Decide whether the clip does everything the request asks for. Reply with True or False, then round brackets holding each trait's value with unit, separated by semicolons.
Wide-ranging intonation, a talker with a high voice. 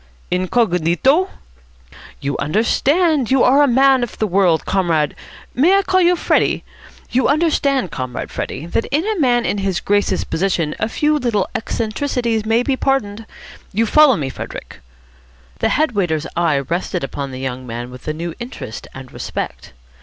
True (8.7 semitones; 215 Hz)